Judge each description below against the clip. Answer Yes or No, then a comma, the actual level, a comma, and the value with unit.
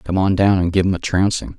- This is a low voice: Yes, very low, 95 Hz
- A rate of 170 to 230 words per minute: No, fast, 305 wpm